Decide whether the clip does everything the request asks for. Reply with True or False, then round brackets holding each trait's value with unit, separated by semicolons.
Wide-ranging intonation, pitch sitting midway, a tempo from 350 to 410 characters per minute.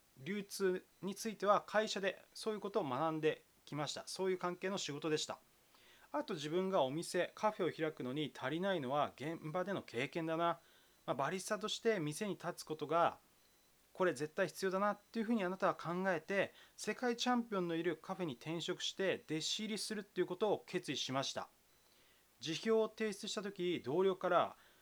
False (4.2 semitones; 180 Hz; 370 characters per minute)